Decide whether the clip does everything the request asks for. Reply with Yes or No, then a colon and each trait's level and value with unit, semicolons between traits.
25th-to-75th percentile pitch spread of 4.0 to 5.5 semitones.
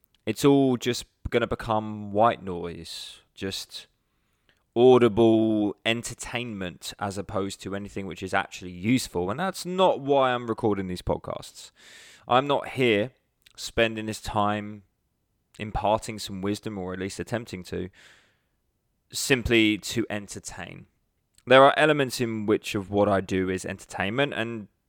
No: average, 3.6 semitones